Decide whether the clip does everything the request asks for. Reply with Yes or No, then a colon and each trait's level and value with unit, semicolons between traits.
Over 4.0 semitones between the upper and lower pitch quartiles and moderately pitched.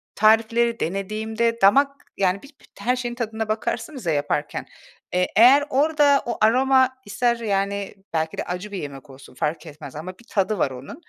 No: average, 4.9 semitones; high, 215 Hz